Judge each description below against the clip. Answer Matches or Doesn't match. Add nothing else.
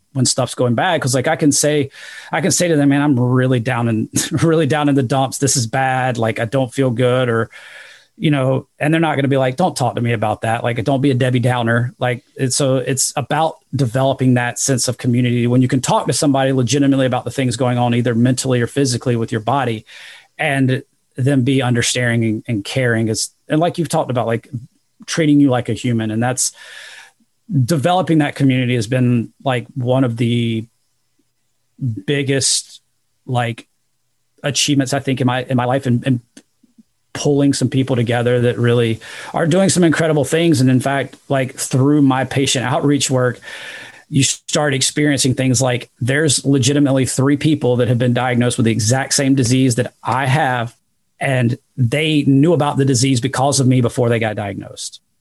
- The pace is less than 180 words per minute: Doesn't match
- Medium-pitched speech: Doesn't match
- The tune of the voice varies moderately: Doesn't match